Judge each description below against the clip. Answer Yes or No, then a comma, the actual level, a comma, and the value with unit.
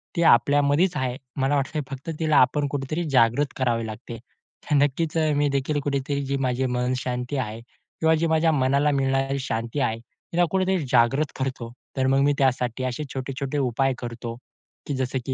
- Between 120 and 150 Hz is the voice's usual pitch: Yes, low, 135 Hz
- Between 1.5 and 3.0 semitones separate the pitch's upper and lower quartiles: Yes, narrow, 2.6 semitones